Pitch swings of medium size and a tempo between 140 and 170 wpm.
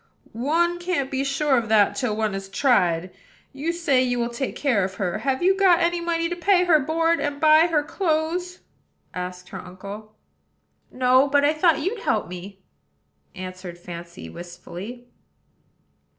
No: wide, 9.0 semitones; average, 165 wpm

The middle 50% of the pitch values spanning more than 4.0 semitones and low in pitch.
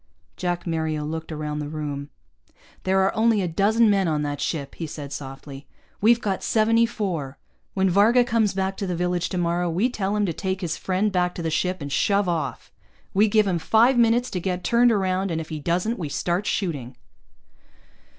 No: average, 4.6 semitones; medium, 185 Hz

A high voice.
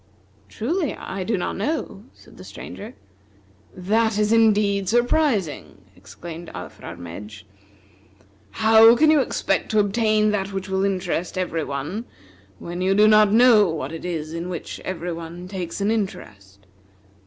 Yes: high, 195 Hz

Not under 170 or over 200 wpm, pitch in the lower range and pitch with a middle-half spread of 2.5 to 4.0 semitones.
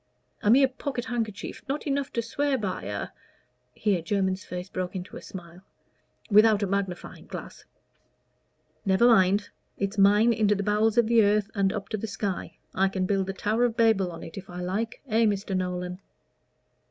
No: average, 185 wpm; high, 205 Hz; average, 2.9 semitones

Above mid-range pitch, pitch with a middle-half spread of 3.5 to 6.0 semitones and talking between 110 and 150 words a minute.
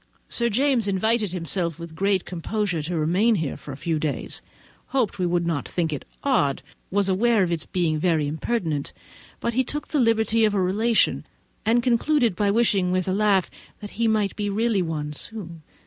No: high, 195 Hz; average, 5.1 semitones; average, 185 wpm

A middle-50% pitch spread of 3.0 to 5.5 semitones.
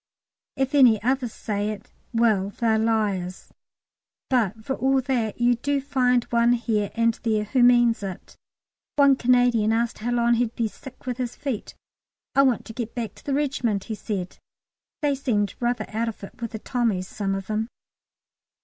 No: narrow, 2.6 semitones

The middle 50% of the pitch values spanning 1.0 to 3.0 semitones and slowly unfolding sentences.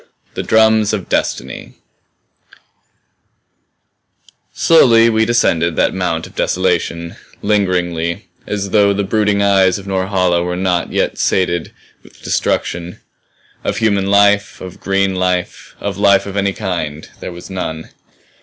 Yes: narrow, 2.5 semitones; slow, 125 wpm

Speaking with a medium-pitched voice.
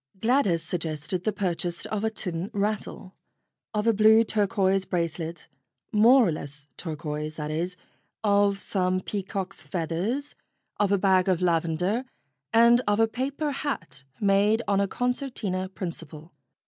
No: high, 195 Hz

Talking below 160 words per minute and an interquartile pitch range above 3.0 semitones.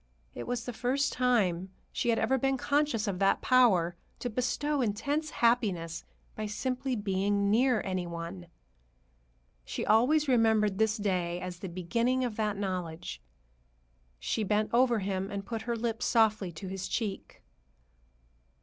Yes: average, 150 wpm; average, 4.6 semitones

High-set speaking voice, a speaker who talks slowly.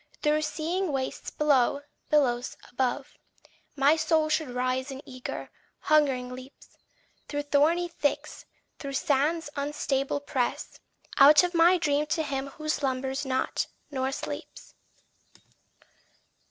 Yes: very high, 285 Hz; slow, 115 wpm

